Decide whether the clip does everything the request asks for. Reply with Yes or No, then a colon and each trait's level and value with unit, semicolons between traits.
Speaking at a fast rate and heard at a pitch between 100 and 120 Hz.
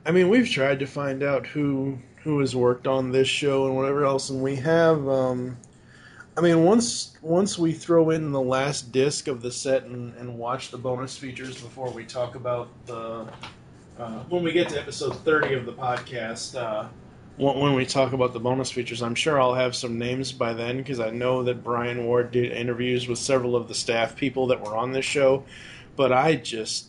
No: fast, 210 wpm; low, 130 Hz